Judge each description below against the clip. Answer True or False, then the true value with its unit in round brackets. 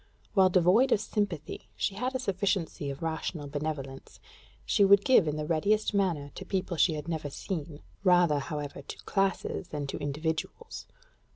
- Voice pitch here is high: False (170 Hz)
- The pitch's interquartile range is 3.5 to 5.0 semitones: True (4.7 semitones)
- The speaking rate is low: False (165 wpm)